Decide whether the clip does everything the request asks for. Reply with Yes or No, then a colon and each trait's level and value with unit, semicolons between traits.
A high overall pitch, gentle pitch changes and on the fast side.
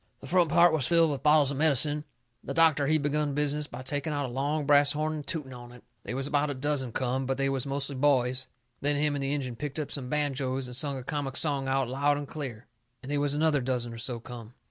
No: medium, 140 Hz; narrow, 2.2 semitones; fast, 255 wpm